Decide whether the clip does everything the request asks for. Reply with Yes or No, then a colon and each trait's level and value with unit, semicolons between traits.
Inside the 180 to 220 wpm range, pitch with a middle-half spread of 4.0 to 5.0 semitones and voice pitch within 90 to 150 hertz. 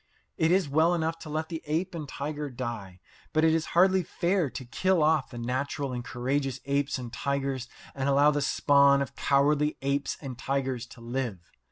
No: average, 190 wpm; average, 3.3 semitones; medium, 140 Hz